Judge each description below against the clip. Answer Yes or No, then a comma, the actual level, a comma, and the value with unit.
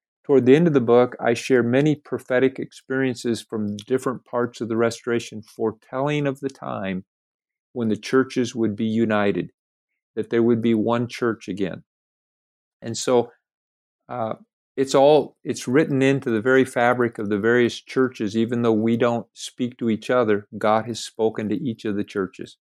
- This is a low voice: Yes, low, 120 Hz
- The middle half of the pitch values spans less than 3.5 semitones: Yes, narrow, 2.6 semitones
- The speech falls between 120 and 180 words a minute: Yes, average, 170 wpm